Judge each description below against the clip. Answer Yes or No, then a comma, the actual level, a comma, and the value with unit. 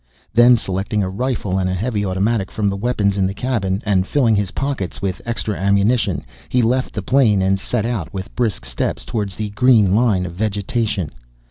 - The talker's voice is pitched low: Yes, low, 105 Hz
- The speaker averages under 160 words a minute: No, average, 195 wpm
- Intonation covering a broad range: No, average, 3.5 semitones